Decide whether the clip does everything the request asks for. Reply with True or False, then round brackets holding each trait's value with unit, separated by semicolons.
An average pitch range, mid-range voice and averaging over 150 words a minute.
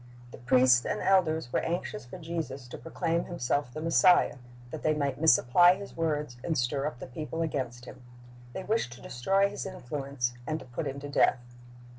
True (5.0 semitones; 145 Hz; 190 wpm)